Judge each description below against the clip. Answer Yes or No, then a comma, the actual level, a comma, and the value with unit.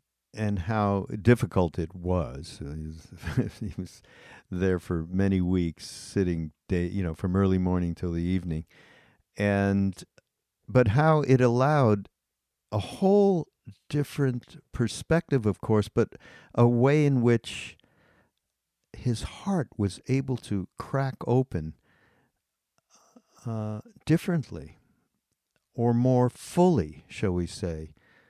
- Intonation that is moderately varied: No, wide, 5.9 semitones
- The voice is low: Yes, low, 105 Hz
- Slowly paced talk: Yes, slow, 110 wpm